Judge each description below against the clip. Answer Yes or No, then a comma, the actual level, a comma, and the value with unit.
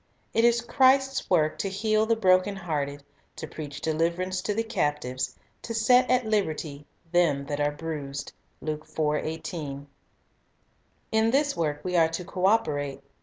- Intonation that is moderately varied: No, wide, 6.9 semitones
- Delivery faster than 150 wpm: No, average, 145 wpm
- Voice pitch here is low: No, medium, 170 Hz